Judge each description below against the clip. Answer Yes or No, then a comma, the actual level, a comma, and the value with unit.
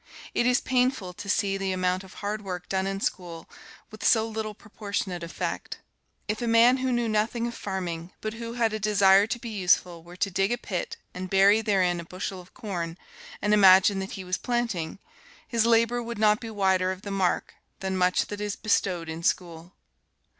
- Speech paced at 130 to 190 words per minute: No, average, 200 wpm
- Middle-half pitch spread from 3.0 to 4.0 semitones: Yes, average, 3.4 semitones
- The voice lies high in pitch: Yes, high, 200 Hz